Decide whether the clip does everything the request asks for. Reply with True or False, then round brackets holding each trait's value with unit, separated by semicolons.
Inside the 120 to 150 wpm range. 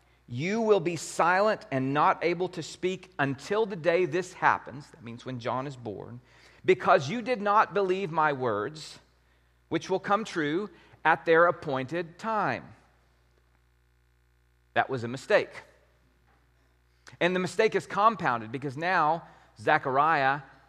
True (135 wpm)